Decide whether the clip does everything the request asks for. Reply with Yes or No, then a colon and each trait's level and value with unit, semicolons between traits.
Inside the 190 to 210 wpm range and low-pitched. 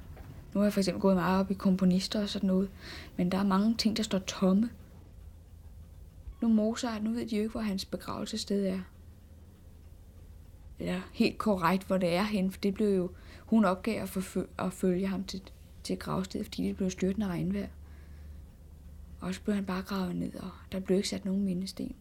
No: average, 200 wpm; medium, 185 Hz